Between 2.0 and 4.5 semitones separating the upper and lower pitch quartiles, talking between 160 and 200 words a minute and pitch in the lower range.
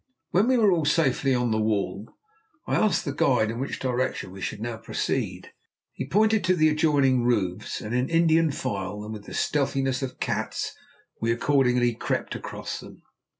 No: wide, 5.6 semitones; average, 180 wpm; low, 130 Hz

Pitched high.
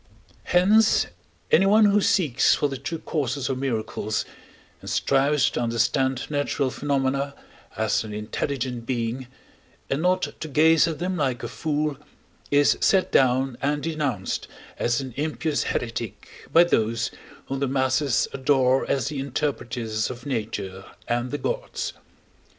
No: low, 135 Hz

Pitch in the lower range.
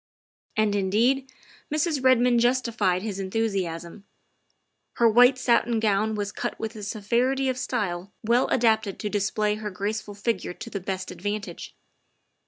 No: high, 215 Hz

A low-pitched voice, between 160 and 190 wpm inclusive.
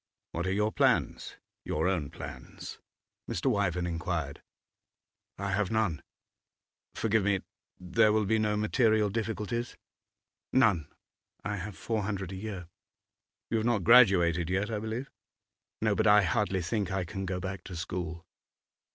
No: low, 100 Hz; average, 145 wpm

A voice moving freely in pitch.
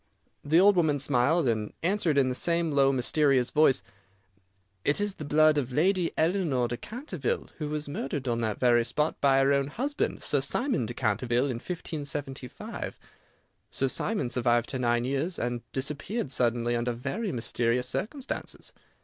No: average, 4.8 semitones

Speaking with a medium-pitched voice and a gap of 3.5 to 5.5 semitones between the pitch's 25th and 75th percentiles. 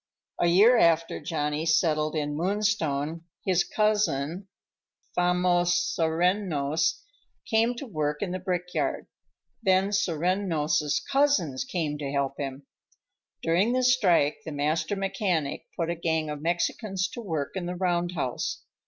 Yes: medium, 170 Hz; average, 4.0 semitones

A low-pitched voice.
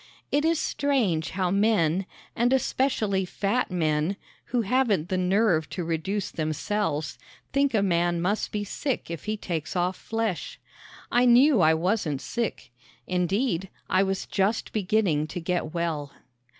No: high, 190 Hz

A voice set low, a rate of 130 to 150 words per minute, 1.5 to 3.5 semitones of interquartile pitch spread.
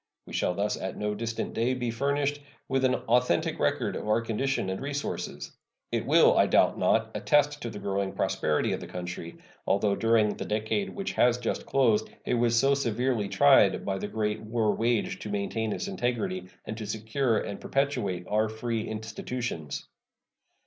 No: low, 110 Hz; average, 175 wpm; average, 3.2 semitones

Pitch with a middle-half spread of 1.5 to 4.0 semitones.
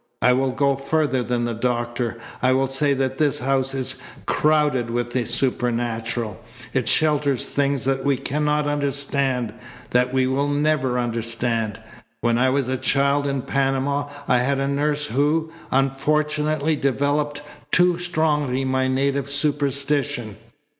Yes: narrow, 2.5 semitones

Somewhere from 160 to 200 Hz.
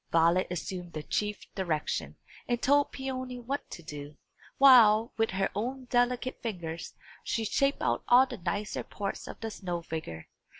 No: high, 210 Hz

